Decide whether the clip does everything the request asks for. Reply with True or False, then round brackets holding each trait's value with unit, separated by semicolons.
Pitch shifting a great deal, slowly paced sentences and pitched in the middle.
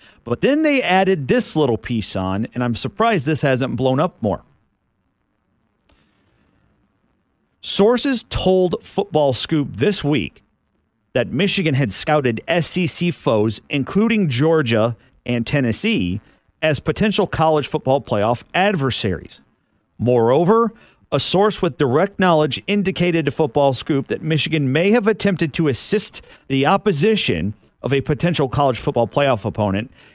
True (7.1 semitones; 125 wpm; 150 Hz)